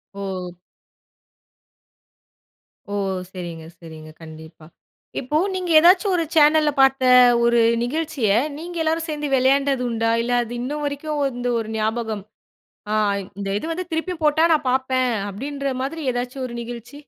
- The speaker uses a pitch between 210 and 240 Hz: No, very high, 260 Hz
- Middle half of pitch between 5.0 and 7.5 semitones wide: Yes, average, 5.3 semitones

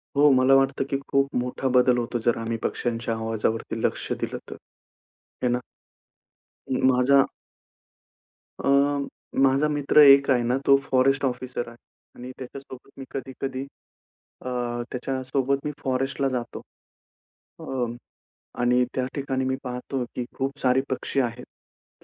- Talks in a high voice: No, low, 130 Hz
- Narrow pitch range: Yes, narrow, 1.7 semitones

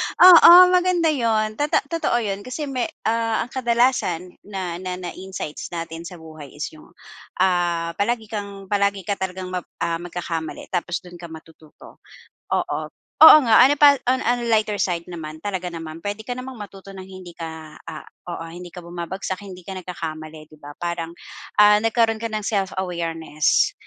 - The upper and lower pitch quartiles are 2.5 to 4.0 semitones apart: No, average, 4.6 semitones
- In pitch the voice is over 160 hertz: Yes, medium, 185 Hz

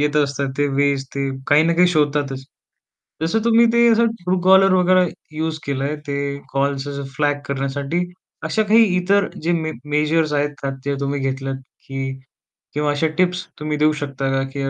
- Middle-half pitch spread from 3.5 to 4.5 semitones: Yes, average, 4.1 semitones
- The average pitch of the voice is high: No, medium, 150 Hz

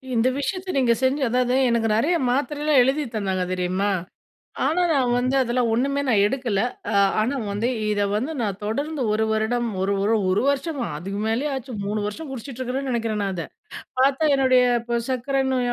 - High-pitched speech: Yes, high, 245 Hz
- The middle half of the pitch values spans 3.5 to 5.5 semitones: Yes, average, 4.0 semitones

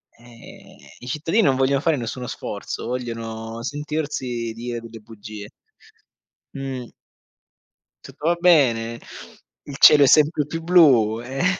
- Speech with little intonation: No, average, 4.3 semitones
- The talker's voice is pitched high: No, low, 125 Hz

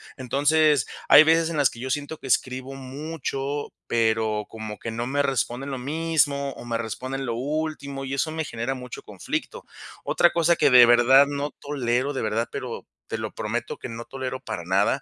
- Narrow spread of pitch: No, average, 3.3 semitones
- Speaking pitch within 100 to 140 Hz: Yes, low, 135 Hz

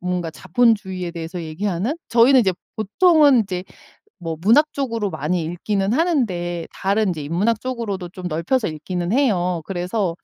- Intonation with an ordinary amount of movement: Yes, average, 5.0 semitones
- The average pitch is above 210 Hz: No, high, 190 Hz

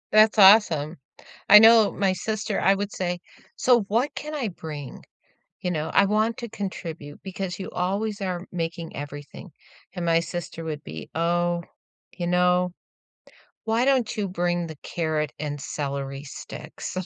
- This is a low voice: No, medium, 180 Hz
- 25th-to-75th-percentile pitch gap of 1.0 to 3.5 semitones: No, average, 4.5 semitones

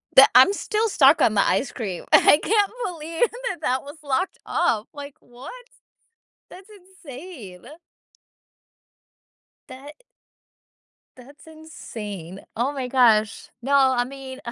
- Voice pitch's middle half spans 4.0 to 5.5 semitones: Yes, average, 5.0 semitones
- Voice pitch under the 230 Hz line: No, very high, 270 Hz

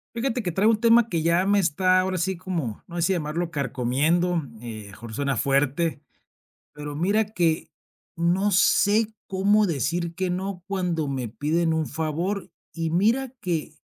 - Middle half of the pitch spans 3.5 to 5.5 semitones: Yes, average, 4.1 semitones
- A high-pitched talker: No, medium, 170 Hz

